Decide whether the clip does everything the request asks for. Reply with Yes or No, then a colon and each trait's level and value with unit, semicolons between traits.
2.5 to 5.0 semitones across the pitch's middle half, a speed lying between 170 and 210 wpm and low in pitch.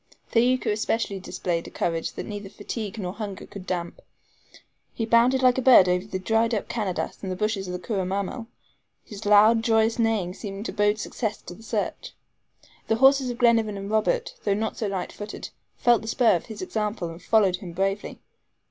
No: average, 2.9 semitones; average, 190 wpm; high, 210 Hz